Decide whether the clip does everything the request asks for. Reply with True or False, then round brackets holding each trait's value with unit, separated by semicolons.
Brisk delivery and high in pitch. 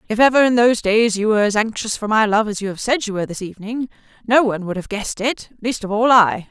True (275 wpm; 220 Hz)